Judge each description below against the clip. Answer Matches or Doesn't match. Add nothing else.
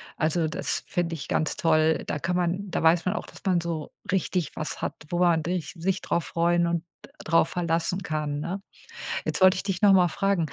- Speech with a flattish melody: Matches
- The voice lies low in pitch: Doesn't match